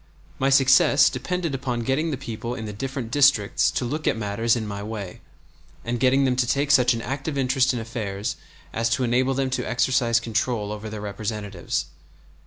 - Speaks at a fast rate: No, average, 190 wpm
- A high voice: No, low, 120 Hz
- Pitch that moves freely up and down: No, average, 3.4 semitones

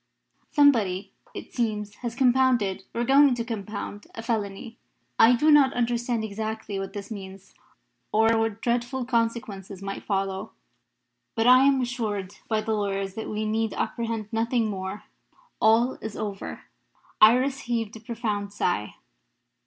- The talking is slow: No, average, 145 wpm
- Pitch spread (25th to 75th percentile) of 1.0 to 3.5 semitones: Yes, average, 2.9 semitones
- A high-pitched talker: Yes, high, 225 Hz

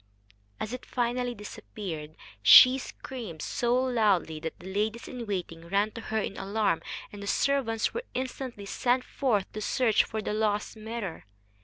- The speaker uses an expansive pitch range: No, average, 3.7 semitones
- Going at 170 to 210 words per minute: No, average, 155 wpm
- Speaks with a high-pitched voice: Yes, high, 215 Hz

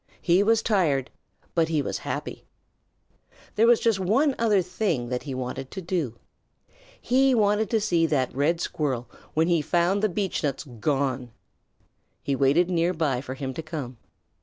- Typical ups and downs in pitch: No, wide, 6.8 semitones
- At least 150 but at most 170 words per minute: Yes, average, 160 wpm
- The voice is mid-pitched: Yes, medium, 165 Hz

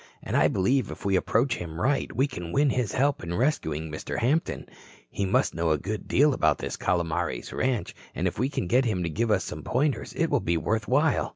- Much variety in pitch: Yes, wide, 7.4 semitones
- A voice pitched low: Yes, low, 110 Hz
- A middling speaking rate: No, fast, 225 wpm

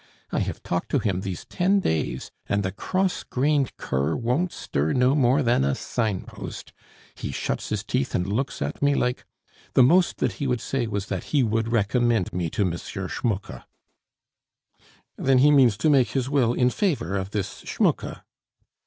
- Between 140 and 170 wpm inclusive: No, average, 180 wpm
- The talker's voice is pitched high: No, low, 120 Hz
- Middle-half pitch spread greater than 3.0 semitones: Yes, wide, 5.6 semitones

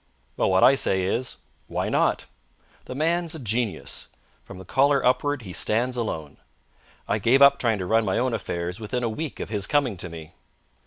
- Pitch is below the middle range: Yes, low, 115 Hz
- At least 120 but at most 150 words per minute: No, average, 195 wpm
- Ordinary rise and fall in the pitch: No, wide, 6.0 semitones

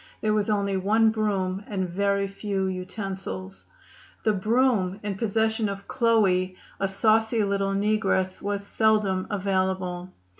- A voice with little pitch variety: Yes, narrow, 2.3 semitones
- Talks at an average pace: No, slow, 125 wpm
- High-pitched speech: Yes, high, 200 Hz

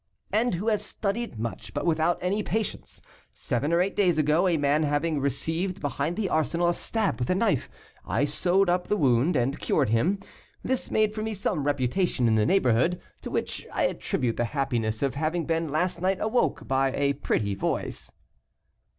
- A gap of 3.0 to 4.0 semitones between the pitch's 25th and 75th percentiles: No, wide, 5.6 semitones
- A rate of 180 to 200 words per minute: Yes, average, 185 wpm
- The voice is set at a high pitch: No, medium, 160 Hz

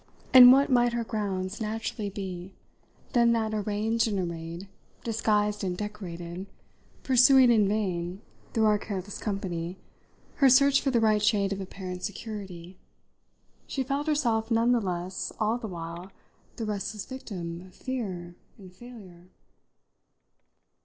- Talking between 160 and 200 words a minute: No, average, 140 wpm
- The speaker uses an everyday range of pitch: Yes, average, 4.0 semitones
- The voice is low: No, high, 210 Hz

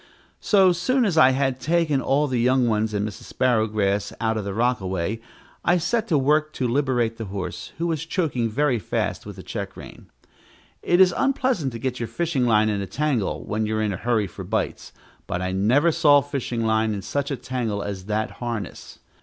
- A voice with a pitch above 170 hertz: No, low, 125 Hz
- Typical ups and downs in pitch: No, wide, 5.8 semitones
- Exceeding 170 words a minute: Yes, fast, 205 wpm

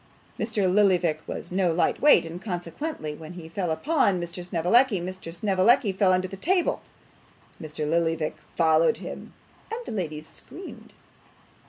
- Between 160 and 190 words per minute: No, average, 145 wpm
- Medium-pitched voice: Yes, medium, 180 Hz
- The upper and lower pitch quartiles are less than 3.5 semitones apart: No, average, 4.0 semitones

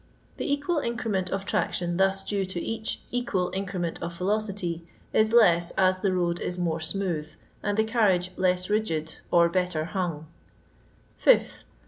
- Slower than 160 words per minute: Yes, average, 145 wpm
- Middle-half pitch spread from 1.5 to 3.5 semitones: Yes, average, 3.2 semitones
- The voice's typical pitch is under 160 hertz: No, medium, 185 Hz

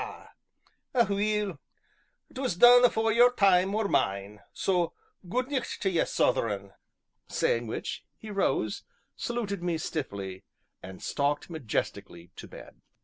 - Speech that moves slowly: Yes, slow, 120 wpm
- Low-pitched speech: No, medium, 180 Hz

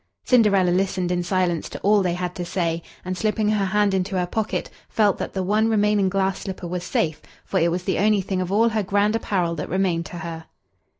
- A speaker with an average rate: No, fast, 225 wpm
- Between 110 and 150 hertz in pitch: No, high, 190 Hz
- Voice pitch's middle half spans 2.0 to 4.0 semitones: Yes, average, 2.8 semitones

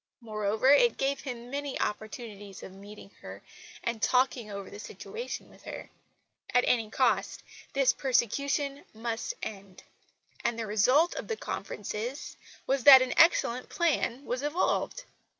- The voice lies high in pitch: Yes, high, 245 Hz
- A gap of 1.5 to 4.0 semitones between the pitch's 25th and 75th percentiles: No, average, 4.5 semitones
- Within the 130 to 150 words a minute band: Yes, average, 140 wpm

